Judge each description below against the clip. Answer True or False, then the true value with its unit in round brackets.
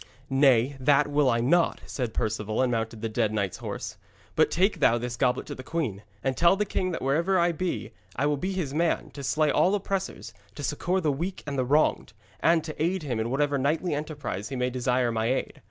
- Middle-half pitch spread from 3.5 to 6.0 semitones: True (5.2 semitones)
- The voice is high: False (140 Hz)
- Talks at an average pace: False (220 wpm)